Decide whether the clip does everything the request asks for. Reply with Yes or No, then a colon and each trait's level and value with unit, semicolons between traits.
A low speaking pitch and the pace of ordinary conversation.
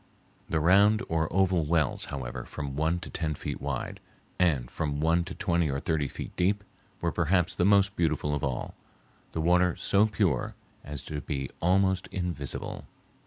Yes: very low, 85 Hz; average, 165 wpm